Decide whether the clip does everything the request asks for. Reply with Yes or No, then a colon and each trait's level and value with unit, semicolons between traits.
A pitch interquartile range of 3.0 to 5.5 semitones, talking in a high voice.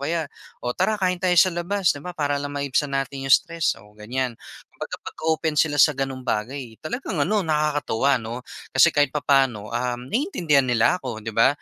No: average, 4.4 semitones; medium, 145 Hz